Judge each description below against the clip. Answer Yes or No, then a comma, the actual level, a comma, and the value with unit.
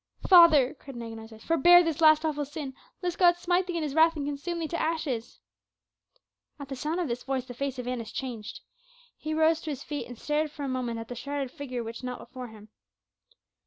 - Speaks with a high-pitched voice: Yes, very high, 285 Hz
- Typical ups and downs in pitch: Yes, average, 4.4 semitones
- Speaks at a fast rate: Yes, fast, 225 wpm